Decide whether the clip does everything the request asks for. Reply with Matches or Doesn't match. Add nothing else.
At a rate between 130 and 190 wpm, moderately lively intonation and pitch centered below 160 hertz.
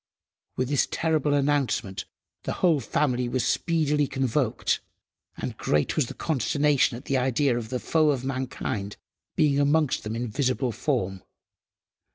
Matches